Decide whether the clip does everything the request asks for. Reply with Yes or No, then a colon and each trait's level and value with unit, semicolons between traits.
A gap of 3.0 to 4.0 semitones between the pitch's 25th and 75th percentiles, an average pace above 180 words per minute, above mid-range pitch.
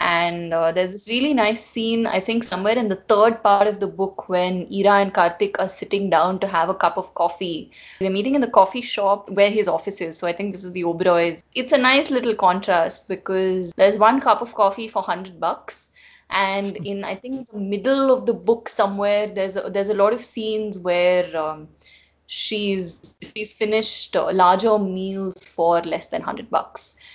Yes: average, 3.3 semitones; average, 200 wpm; high, 200 Hz